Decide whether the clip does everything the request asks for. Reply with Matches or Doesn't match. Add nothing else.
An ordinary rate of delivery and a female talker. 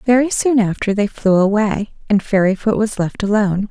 Matches